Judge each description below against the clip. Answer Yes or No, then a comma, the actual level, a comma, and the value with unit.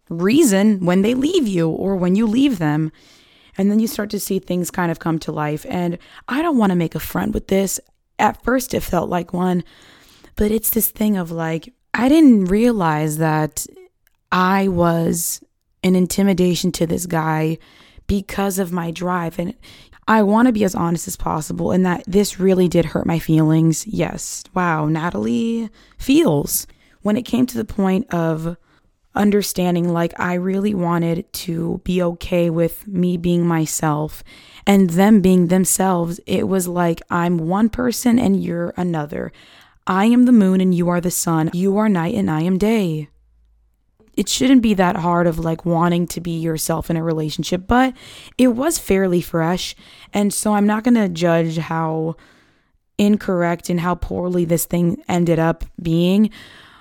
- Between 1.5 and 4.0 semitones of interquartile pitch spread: Yes, average, 3.5 semitones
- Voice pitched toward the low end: No, medium, 180 Hz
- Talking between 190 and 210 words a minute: No, average, 175 wpm